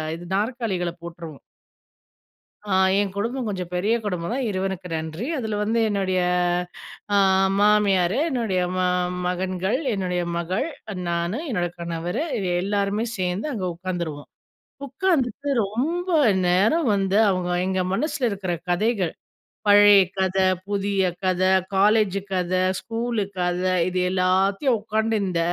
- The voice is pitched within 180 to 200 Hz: Yes, high, 195 Hz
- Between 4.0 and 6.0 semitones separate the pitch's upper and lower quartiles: No, average, 3.5 semitones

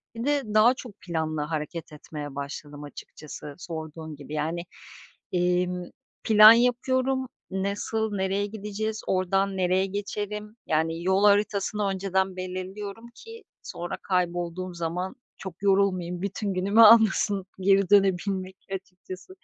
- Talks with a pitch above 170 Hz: Yes, high, 190 Hz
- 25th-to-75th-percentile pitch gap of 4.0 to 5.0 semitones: No, average, 2.9 semitones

